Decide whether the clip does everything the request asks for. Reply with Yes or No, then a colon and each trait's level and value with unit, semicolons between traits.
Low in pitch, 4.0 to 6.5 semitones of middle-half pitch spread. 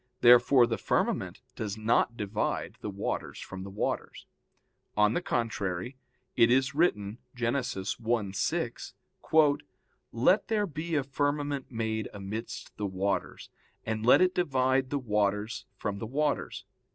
Yes: low, 115 Hz; average, 5.1 semitones